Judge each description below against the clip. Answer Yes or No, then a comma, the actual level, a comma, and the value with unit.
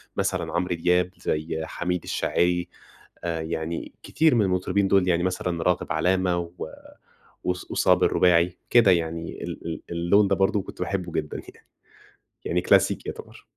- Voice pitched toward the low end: Yes, very low, 90 Hz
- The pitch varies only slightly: Yes, narrow, 1.7 semitones